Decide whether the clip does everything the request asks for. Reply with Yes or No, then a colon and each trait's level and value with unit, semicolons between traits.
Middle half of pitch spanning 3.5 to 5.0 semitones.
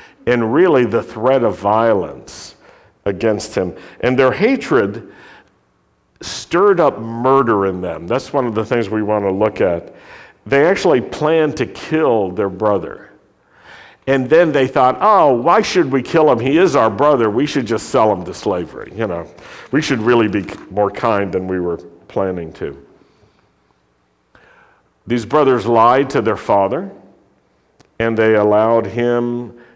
Yes: average, 4.7 semitones